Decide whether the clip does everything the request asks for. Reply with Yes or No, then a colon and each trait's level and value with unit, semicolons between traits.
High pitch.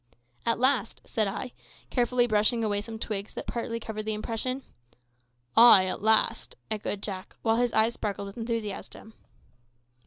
Yes: high, 220 Hz